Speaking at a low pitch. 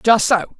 No: high, 215 Hz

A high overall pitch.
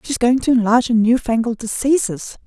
Yes: high, 240 Hz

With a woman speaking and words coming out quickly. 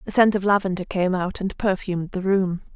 Yes: female; fast, 220 wpm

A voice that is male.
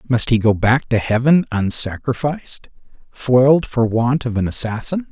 Yes: male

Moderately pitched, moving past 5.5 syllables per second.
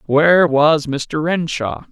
No: medium, 155 Hz; 3.4 syllables/s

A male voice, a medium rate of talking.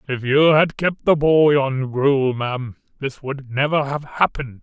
Yes: male; average, 180 wpm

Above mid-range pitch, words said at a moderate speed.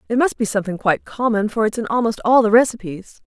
No: high, 225 Hz; fast, 240 wpm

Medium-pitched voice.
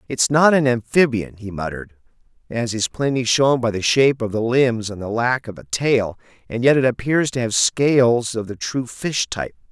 No: low, 120 Hz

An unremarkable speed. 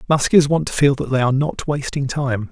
No: fast, 240 wpm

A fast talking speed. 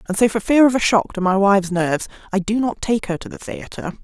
Yes: fast, 280 wpm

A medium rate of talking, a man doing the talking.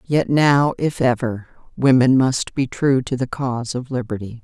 No: average, 175 wpm; female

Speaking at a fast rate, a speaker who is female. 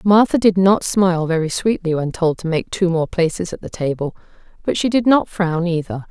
Yes: fast, 215 wpm; female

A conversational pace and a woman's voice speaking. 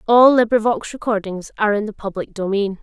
Yes: average, 170 wpm; female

